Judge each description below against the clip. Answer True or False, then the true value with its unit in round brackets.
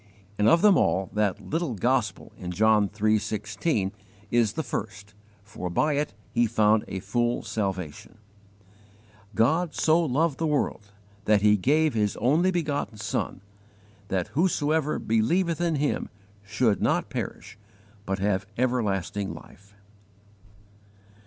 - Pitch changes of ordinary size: False (6.6 semitones)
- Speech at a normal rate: False (130 wpm)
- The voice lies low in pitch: True (110 Hz)